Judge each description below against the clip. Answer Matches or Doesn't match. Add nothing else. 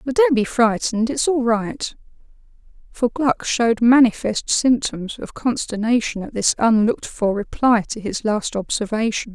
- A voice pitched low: Doesn't match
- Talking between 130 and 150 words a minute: Matches